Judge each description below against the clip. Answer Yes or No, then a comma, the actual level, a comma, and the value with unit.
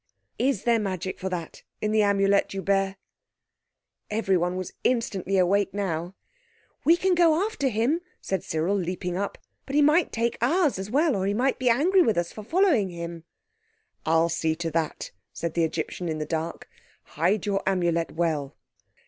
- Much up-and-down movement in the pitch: Yes, wide, 5.7 semitones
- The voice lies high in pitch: Yes, high, 195 Hz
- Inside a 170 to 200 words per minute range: Yes, average, 175 wpm